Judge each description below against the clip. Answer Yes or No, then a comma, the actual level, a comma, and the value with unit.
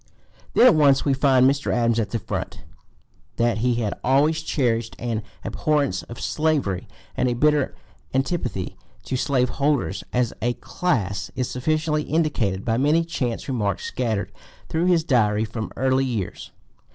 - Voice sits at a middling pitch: No, low, 125 Hz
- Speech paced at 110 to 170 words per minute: Yes, average, 150 wpm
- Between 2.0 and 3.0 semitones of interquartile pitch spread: No, average, 4.6 semitones